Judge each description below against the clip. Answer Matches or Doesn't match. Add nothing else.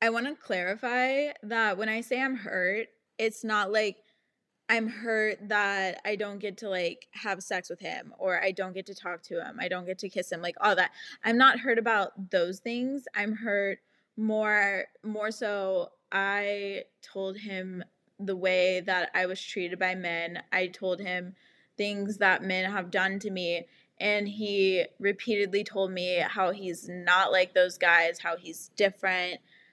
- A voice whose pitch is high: Matches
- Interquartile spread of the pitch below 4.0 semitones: Matches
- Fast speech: Doesn't match